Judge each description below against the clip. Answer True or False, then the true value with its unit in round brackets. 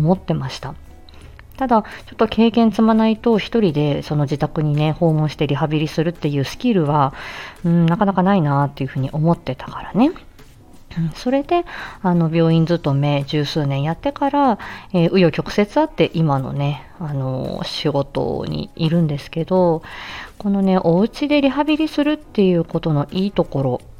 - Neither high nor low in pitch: True (165 Hz)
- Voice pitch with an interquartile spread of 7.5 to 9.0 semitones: False (6.2 semitones)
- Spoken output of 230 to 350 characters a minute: True (345 characters per minute)